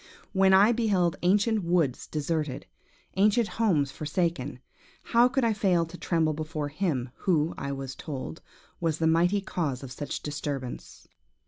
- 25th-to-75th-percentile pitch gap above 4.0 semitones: Yes, average, 4.9 semitones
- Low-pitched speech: No, medium, 165 Hz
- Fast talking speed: No, average, 145 wpm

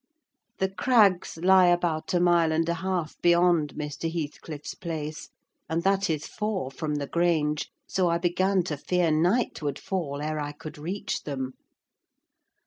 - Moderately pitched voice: Yes, medium, 170 Hz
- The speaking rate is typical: Yes, average, 155 wpm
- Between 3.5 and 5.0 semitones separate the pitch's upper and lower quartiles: No, average, 3.0 semitones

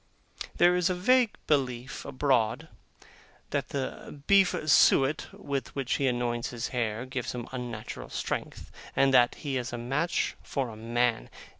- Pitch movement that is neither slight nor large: Yes, average, 3.1 semitones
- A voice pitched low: Yes, low, 130 Hz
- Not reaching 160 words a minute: Yes, average, 150 wpm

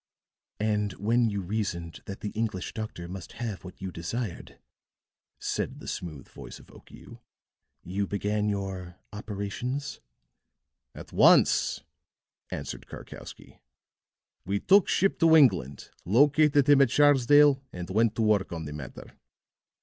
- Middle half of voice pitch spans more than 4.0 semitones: Yes, average, 5.1 semitones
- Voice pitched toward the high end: No, low, 105 Hz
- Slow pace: Yes, slow, 130 wpm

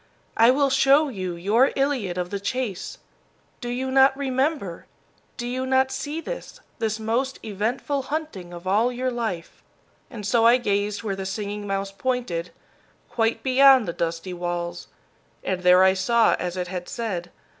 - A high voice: Yes, high, 225 Hz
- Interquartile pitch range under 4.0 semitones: No, wide, 5.6 semitones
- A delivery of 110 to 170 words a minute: Yes, average, 165 wpm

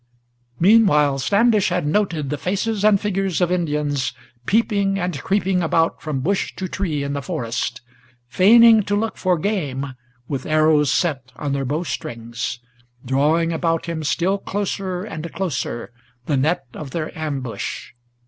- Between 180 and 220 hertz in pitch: No, medium, 165 Hz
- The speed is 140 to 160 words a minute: Yes, average, 150 wpm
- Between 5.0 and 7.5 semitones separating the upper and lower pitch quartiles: Yes, wide, 5.6 semitones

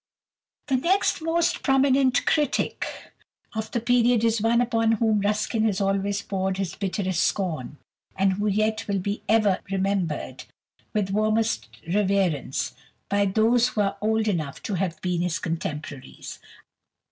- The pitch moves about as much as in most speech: Yes, average, 3.1 semitones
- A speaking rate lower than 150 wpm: Yes, average, 140 wpm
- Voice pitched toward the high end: Yes, high, 205 Hz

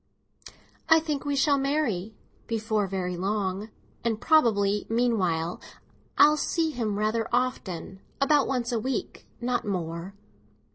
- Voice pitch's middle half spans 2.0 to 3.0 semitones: No, wide, 5.5 semitones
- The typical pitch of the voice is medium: No, high, 225 Hz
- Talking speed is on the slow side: Yes, slow, 125 wpm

